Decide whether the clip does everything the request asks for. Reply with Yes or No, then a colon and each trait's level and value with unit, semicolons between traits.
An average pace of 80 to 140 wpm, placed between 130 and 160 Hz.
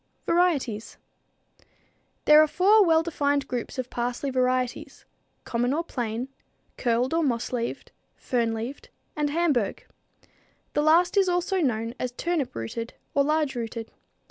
No: slow, 135 wpm; very high, 265 Hz